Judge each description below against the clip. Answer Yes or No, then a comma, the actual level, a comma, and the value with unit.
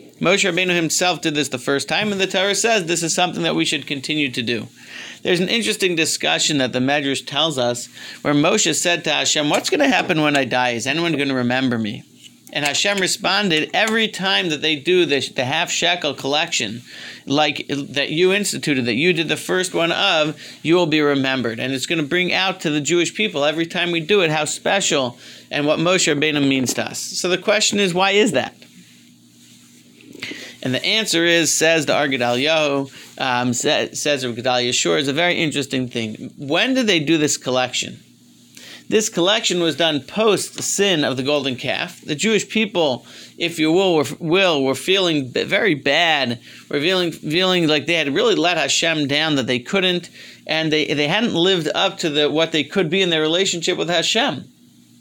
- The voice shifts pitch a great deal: No, average, 4.8 semitones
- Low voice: No, medium, 155 Hz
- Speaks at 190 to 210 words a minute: Yes, average, 195 wpm